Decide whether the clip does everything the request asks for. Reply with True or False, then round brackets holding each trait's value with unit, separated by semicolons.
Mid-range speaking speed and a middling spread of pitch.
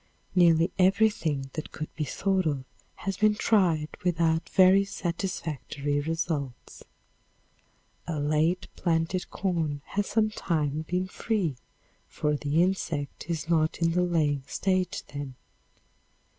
False (115 wpm; 3.6 semitones)